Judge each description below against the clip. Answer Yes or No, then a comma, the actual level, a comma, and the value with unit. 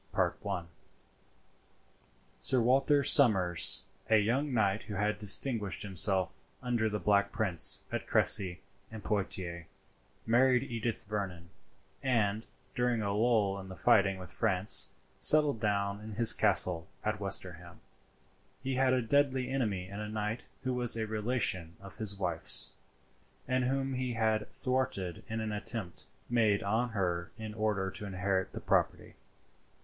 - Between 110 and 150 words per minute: Yes, average, 140 wpm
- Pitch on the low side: Yes, low, 105 Hz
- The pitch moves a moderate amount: Yes, average, 3.7 semitones